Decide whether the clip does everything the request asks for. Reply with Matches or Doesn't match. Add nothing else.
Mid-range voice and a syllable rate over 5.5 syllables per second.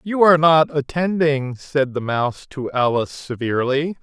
Doesn't match